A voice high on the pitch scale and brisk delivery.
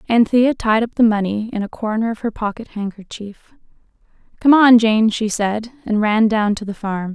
No: high, 220 Hz; average, 195 wpm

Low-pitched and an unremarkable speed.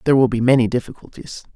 Yes: low, 125 Hz; average, 195 wpm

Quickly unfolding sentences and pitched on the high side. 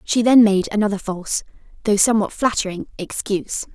No: average, 145 wpm; high, 205 Hz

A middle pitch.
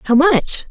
No: very high, 290 Hz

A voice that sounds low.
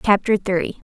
No: high, 195 Hz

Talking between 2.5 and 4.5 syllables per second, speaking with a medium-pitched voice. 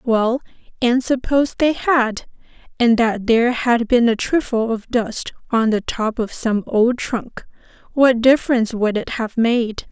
No: 4.2 syllables/s; high, 235 Hz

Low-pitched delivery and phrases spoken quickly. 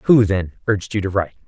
Yes: low, 100 Hz; fast, 245 wpm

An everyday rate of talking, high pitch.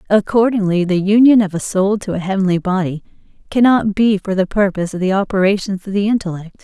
Yes: average, 190 wpm; high, 195 Hz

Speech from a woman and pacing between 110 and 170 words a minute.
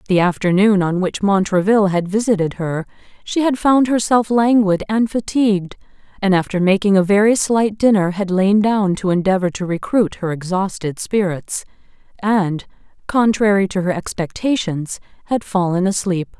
Yes: female; average, 145 wpm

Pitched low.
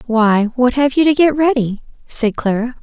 No: very high, 250 Hz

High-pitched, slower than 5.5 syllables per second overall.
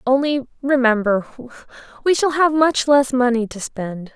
Yes: very high, 255 Hz; 4.3 syllables/s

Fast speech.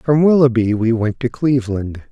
No: average, 170 wpm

